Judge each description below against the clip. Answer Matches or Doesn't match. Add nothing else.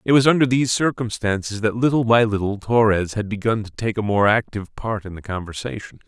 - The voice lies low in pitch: Matches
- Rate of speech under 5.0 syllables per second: Doesn't match